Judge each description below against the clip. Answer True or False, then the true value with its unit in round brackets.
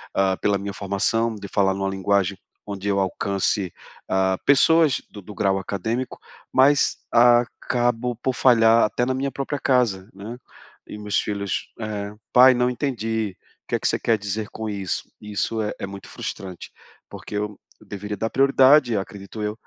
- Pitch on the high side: False (105 Hz)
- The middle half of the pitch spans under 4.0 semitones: True (3.6 semitones)